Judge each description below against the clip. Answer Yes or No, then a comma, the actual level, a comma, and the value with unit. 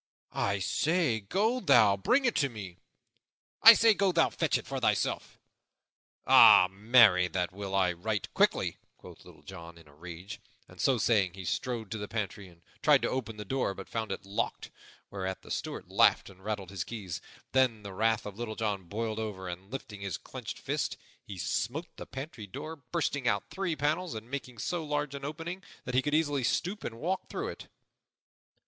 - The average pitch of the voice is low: Yes, low, 110 Hz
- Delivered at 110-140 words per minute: No, average, 190 wpm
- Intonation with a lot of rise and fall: Yes, wide, 6.6 semitones